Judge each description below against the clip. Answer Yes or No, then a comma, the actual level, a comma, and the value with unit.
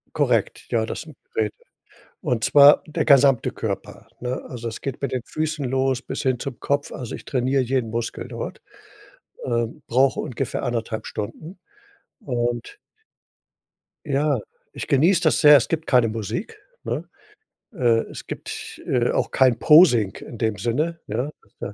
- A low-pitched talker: Yes, low, 130 Hz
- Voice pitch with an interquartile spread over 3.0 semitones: Yes, average, 3.8 semitones